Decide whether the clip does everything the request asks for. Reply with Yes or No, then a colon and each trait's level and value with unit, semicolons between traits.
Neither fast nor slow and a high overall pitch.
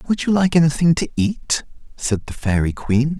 No: average, 190 wpm; medium, 145 Hz